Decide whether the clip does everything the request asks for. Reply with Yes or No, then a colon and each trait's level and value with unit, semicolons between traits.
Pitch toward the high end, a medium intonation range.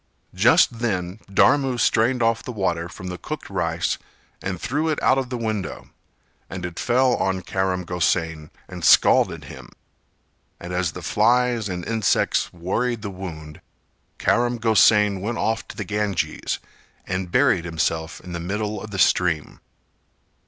No: low, 100 Hz; average, 4.6 semitones